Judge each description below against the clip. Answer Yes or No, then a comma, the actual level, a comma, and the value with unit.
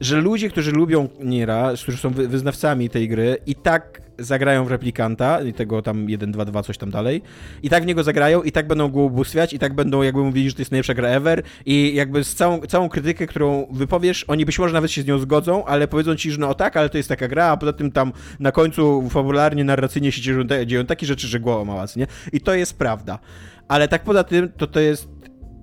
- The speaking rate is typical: No, fast, 235 wpm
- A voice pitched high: No, medium, 140 Hz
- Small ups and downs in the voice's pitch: No, average, 3.7 semitones